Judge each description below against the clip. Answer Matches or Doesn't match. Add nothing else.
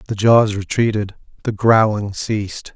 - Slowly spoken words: Matches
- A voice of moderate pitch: Doesn't match